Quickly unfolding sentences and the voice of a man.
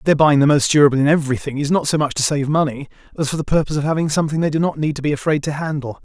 Yes: fast, 300 wpm; male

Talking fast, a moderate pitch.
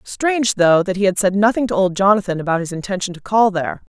No: fast, 240 wpm; high, 195 Hz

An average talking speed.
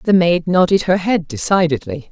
Yes: average, 170 wpm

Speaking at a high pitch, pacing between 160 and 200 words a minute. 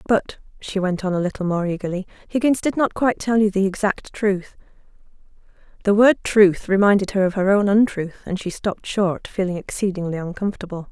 Yes: high, 195 Hz; average, 180 wpm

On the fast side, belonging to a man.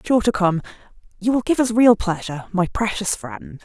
No: fast, 215 wpm; female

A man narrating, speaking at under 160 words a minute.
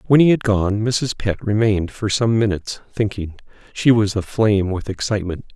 No: male; average, 175 wpm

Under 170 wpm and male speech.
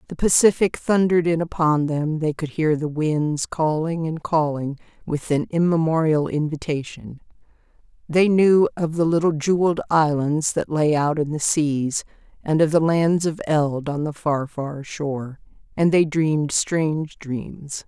No: average, 160 wpm; female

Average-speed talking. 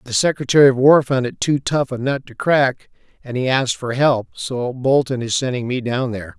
No: fast, 225 wpm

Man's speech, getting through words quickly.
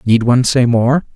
Yes: male; fast, 210 wpm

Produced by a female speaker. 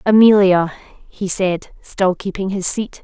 Yes: female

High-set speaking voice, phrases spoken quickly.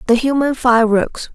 No: high, 245 Hz; slow, 135 wpm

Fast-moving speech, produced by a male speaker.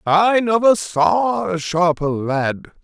No: slow, 125 wpm; male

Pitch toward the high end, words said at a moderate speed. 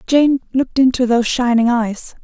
Yes: high, 245 Hz; average, 160 wpm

